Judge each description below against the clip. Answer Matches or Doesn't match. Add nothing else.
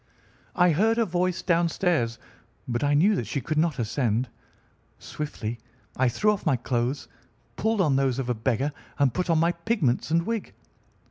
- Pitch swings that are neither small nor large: Doesn't match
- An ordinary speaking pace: Matches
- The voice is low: Doesn't match